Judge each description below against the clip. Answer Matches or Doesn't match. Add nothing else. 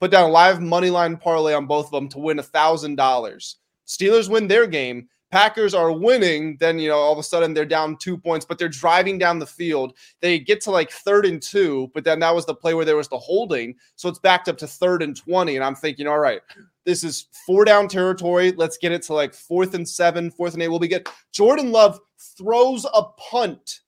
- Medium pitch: Matches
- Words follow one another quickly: Matches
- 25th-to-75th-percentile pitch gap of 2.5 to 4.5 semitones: Matches